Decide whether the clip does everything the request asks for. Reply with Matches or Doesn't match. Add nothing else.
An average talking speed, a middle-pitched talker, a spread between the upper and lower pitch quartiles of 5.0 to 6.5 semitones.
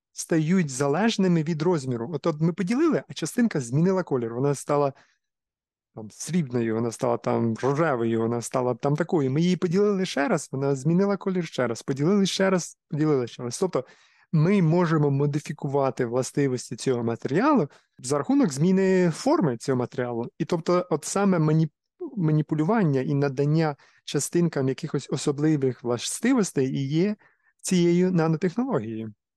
Matches